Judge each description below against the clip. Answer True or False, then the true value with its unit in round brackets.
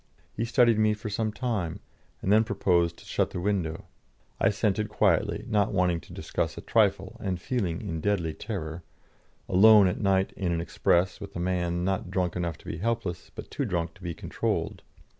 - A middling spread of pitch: True (3.5 semitones)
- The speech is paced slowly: False (190 wpm)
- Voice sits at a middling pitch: False (95 Hz)